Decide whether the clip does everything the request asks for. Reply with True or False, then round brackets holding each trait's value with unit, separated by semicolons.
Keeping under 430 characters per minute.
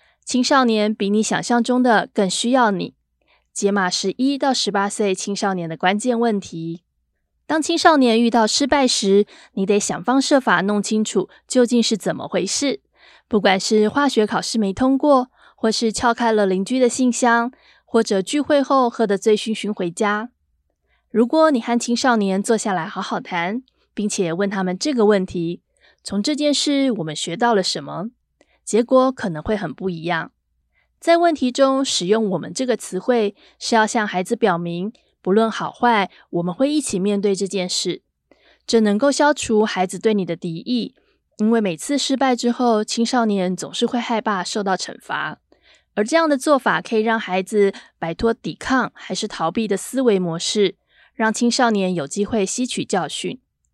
True (255 characters per minute)